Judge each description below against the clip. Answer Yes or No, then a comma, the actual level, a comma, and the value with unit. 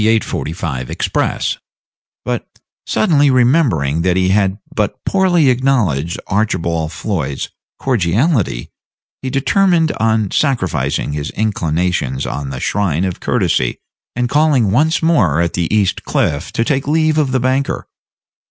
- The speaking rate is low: Yes, slow, 125 wpm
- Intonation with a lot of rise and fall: Yes, wide, 8.5 semitones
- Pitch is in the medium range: No, low, 105 Hz